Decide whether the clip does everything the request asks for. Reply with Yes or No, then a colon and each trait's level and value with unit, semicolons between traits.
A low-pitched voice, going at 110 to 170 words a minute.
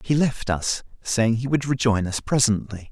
No: low, 120 Hz; average, 185 wpm